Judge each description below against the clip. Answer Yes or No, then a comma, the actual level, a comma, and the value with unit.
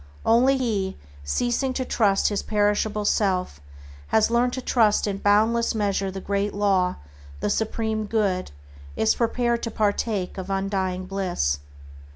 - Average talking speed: Yes, average, 145 wpm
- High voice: Yes, high, 205 Hz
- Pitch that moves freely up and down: No, average, 2.8 semitones